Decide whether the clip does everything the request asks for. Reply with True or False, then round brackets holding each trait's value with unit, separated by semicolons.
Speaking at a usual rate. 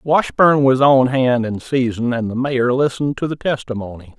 True (185 wpm)